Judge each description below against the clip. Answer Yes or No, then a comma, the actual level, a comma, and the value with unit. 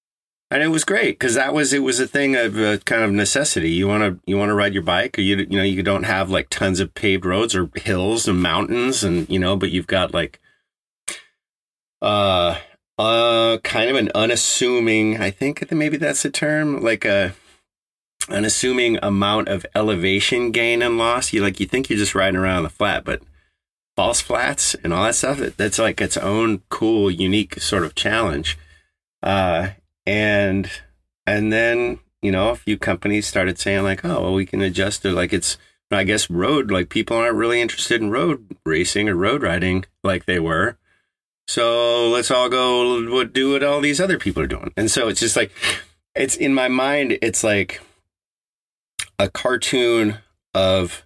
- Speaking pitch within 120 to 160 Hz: No, low, 105 Hz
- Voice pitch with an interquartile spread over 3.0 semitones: Yes, average, 3.6 semitones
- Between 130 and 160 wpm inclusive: No, average, 190 wpm